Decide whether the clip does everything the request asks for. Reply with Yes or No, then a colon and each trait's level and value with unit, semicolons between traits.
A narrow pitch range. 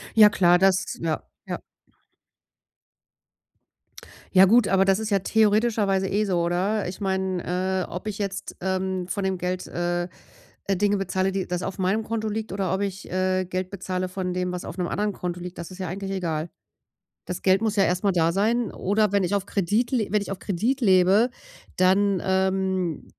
Yes: narrow, 1.9 semitones